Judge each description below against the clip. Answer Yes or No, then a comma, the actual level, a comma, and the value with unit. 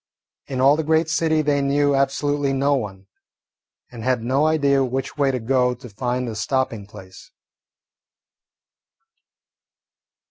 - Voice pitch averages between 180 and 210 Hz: No, low, 135 Hz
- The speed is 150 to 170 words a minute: No, slow, 135 wpm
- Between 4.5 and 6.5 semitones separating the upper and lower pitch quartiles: No, average, 2.7 semitones